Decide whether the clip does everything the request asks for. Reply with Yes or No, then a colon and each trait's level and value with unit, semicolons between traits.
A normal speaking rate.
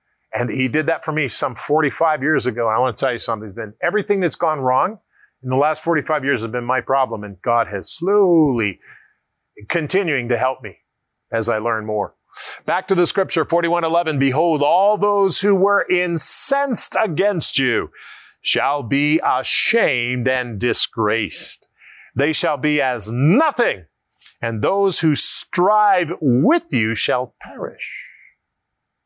Yes: average, 155 wpm